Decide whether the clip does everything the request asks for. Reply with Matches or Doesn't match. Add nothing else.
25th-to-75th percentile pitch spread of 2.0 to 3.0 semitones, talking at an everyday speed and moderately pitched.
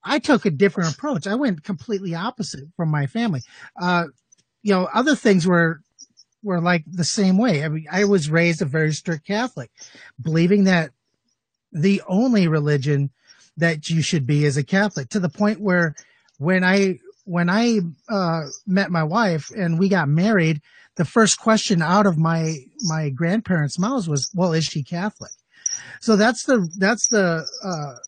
Doesn't match